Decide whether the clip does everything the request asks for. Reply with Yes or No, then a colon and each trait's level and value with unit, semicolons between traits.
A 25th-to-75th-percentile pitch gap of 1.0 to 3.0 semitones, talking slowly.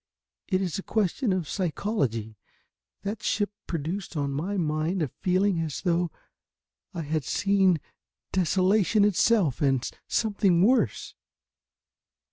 No: average, 4.6 semitones; slow, 115 wpm